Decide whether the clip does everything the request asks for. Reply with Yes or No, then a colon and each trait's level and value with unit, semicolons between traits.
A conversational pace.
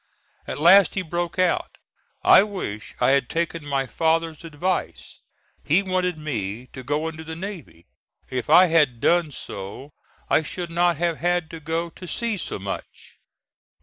Yes: average, 160 wpm